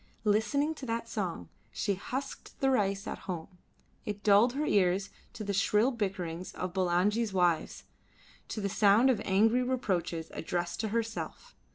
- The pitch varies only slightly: No, average, 4.0 semitones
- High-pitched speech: Yes, high, 205 Hz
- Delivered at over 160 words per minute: No, average, 155 wpm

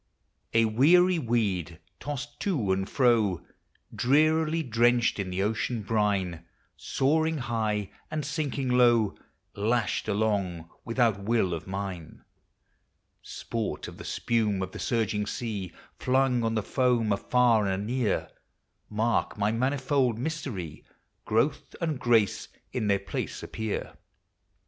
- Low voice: Yes, low, 115 Hz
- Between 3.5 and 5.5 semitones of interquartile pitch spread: Yes, average, 4.2 semitones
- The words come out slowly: Yes, slow, 125 wpm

